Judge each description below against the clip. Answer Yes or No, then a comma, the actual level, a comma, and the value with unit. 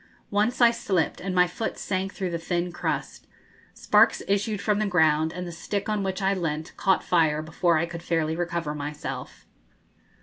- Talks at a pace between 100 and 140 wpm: No, average, 180 wpm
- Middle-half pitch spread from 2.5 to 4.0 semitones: Yes, average, 3.4 semitones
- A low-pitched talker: No, medium, 180 Hz